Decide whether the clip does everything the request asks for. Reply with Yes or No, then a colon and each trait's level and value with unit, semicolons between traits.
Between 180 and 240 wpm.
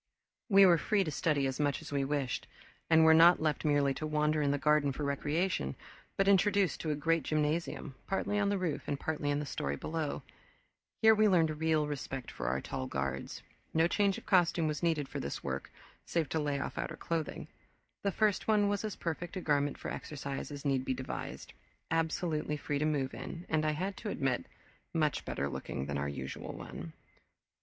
Yes: average, 200 wpm